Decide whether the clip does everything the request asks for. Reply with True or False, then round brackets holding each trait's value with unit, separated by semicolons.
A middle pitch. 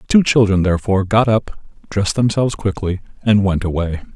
False (100 Hz)